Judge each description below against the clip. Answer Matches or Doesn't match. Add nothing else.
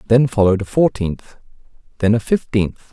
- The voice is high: Doesn't match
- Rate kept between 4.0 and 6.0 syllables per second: Matches